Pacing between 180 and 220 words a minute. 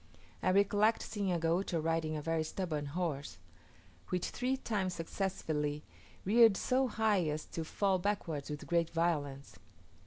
No: average, 145 wpm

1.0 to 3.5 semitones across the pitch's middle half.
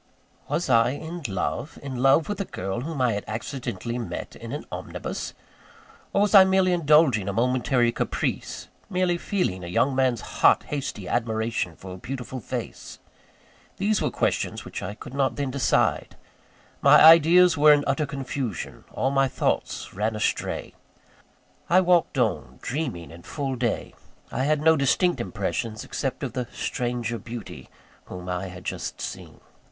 No: wide, 5.4 semitones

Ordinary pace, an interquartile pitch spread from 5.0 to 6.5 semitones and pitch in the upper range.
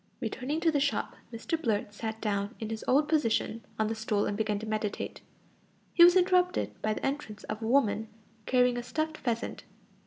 Yes: average, 190 wpm; average, 5.3 semitones; high, 230 Hz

